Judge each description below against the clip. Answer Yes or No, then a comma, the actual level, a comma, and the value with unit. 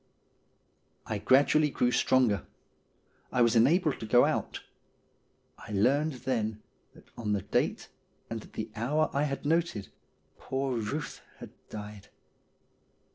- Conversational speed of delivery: No, slow, 130 wpm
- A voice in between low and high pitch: No, low, 120 Hz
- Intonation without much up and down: No, average, 4.7 semitones